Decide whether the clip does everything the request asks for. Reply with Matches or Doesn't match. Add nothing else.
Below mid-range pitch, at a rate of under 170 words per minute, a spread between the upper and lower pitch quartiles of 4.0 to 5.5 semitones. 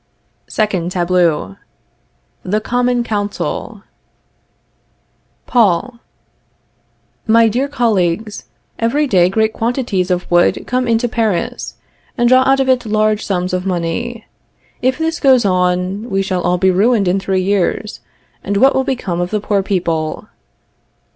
Doesn't match